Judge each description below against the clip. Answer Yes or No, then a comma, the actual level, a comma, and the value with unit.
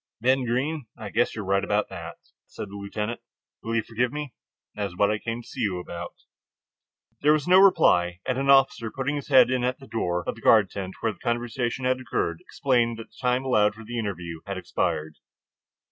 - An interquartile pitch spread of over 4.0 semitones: Yes, average, 4.5 semitones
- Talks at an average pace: No, fast, 220 wpm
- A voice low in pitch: Yes, low, 115 Hz